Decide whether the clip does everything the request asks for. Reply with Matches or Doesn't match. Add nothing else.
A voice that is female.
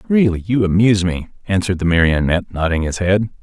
Doesn't match